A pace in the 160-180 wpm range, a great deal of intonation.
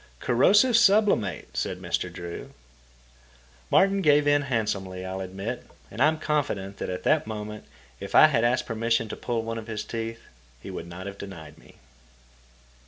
Yes: average, 170 wpm; wide, 7.0 semitones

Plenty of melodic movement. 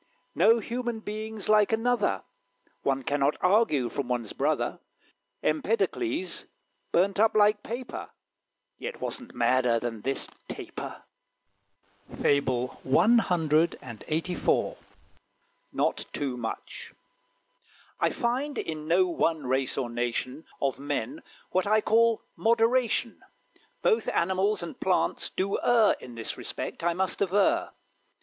Yes: wide, 8.6 semitones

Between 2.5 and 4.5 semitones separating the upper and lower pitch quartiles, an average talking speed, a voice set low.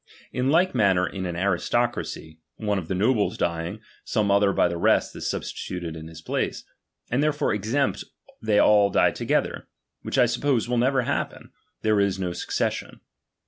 No: average, 5.2 semitones; average, 170 wpm; low, 100 Hz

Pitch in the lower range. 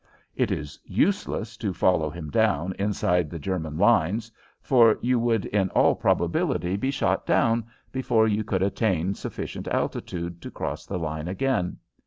Yes: very low, 95 Hz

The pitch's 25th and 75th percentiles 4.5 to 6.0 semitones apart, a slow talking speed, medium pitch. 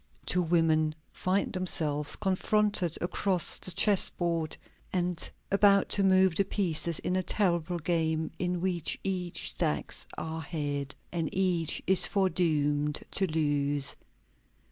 No: average, 3.1 semitones; slow, 120 wpm; medium, 175 Hz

